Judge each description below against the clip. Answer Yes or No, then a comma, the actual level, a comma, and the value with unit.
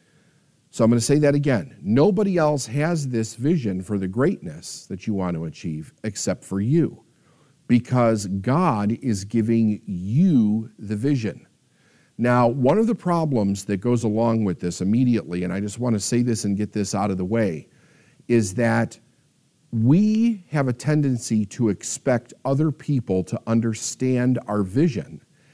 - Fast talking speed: No, average, 160 wpm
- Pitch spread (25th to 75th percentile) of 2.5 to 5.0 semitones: No, wide, 5.5 semitones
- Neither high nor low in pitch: No, low, 120 Hz